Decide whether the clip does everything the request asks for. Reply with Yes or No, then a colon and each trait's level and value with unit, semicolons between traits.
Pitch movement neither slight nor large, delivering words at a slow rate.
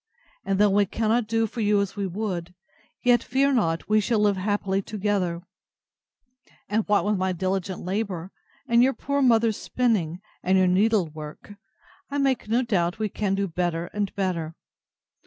No: average, 3.3 semitones; average, 170 wpm